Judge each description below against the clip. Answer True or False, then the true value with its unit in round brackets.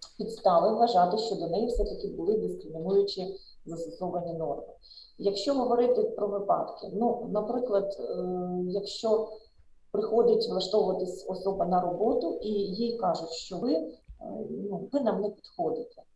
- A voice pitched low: False (205 Hz)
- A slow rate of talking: False (125 wpm)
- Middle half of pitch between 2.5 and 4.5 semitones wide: True (4.0 semitones)